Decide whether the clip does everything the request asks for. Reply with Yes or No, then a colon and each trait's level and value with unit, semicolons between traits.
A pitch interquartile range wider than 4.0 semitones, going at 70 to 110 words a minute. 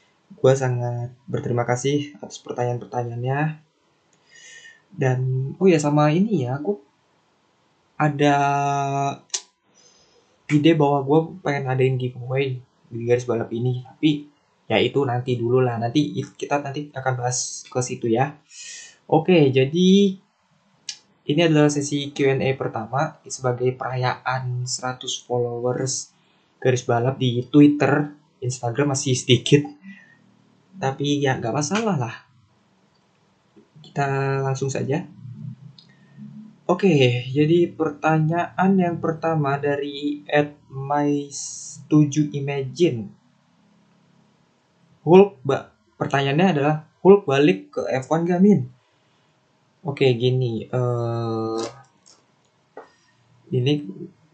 No: average, 3.7 semitones; average, 100 wpm